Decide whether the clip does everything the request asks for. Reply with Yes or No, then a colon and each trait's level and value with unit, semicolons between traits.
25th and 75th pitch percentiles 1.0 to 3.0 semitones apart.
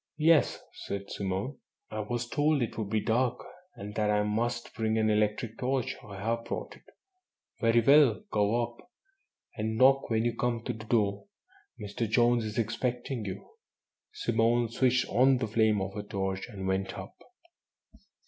Yes: narrow, 2.6 semitones